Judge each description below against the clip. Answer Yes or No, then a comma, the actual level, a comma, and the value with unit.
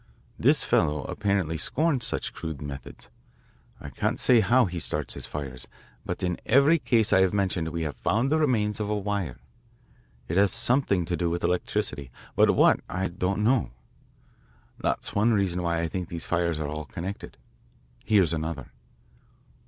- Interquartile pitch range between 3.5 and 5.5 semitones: Yes, average, 4.5 semitones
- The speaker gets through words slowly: No, average, 170 wpm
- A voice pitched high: No, very low, 90 Hz